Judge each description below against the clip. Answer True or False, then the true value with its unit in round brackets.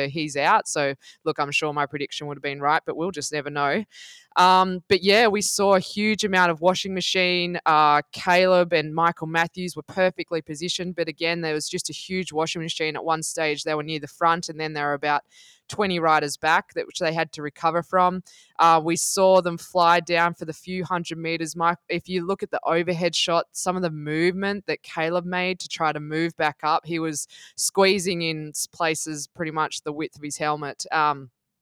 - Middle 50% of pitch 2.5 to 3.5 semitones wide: True (2.9 semitones)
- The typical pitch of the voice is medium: True (165 Hz)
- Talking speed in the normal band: False (215 wpm)